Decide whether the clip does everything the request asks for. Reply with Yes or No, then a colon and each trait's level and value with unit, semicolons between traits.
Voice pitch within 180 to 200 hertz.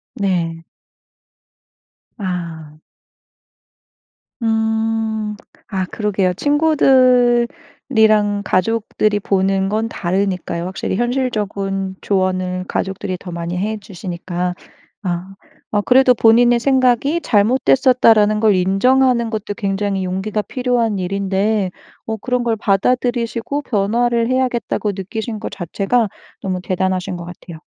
No: high, 210 Hz